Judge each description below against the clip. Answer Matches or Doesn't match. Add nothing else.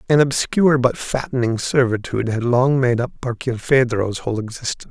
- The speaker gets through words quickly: Doesn't match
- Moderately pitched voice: Doesn't match